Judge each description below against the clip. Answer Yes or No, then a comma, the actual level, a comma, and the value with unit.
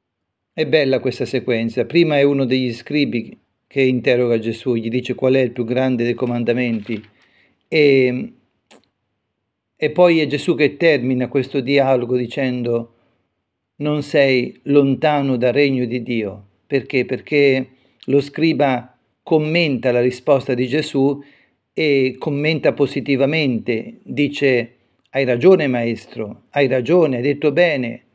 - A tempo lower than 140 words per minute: Yes, average, 125 wpm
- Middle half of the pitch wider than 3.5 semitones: No, average, 3.0 semitones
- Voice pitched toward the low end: Yes, low, 130 Hz